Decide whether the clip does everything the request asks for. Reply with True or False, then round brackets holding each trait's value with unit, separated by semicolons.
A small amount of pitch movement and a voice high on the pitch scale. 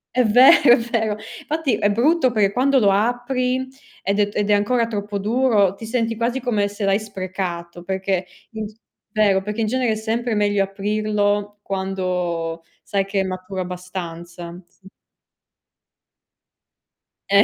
False (3.2 semitones; 205 Hz)